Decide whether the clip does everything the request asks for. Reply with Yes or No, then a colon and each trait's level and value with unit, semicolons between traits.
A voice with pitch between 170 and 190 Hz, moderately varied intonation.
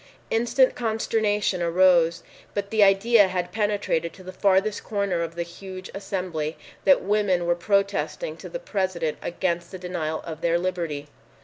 Yes: medium, 185 Hz; average, 3.0 semitones